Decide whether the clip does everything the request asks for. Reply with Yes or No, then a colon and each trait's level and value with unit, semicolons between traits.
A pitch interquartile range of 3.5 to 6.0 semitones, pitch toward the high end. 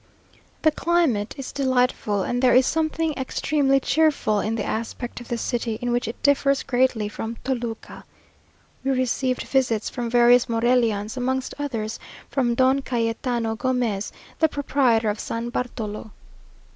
No: average, 2.8 semitones; high, 245 Hz